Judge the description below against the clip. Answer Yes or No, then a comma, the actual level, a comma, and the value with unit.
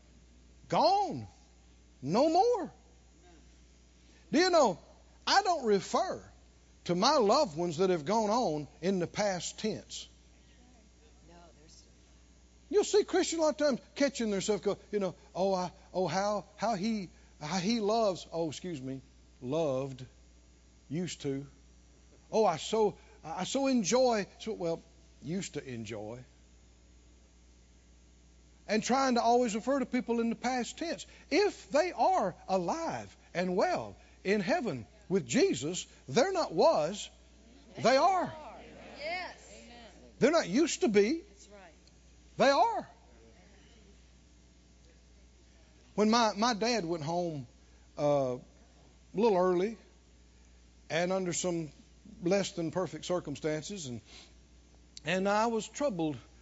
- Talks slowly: Yes, slow, 120 wpm